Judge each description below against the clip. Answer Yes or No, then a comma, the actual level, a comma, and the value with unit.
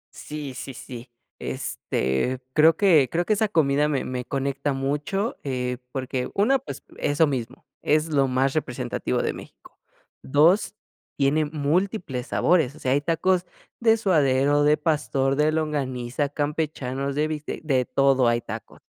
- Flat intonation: No, average, 3.1 semitones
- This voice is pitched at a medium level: Yes, medium, 145 Hz